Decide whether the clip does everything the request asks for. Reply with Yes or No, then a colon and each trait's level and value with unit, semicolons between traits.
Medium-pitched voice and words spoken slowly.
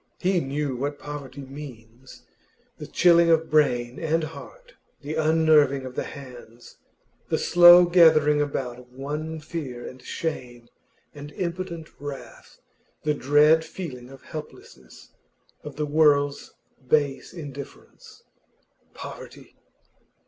Yes: medium, 145 Hz; slow, 115 wpm